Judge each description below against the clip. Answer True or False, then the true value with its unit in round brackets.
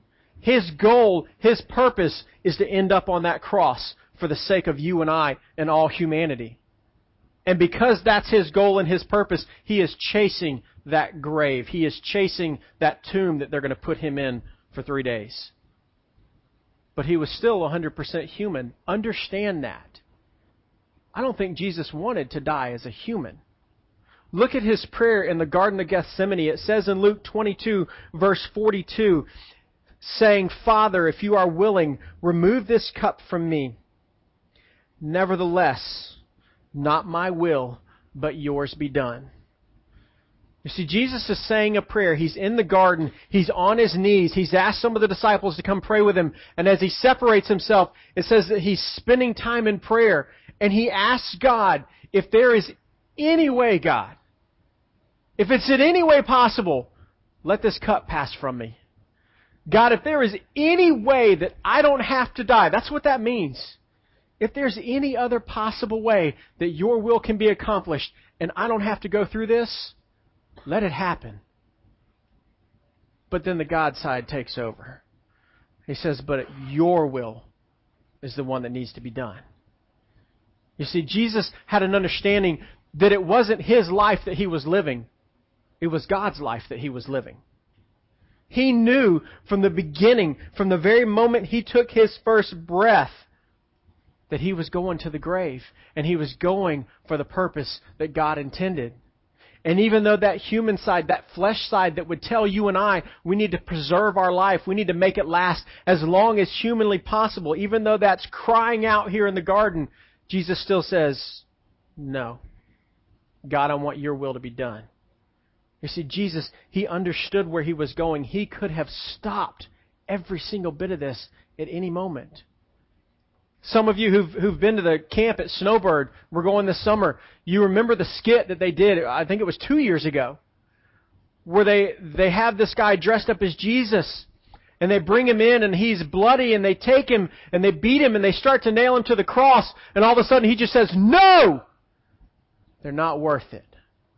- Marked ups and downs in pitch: True (7.0 semitones)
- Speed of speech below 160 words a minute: False (180 wpm)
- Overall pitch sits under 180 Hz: False (185 Hz)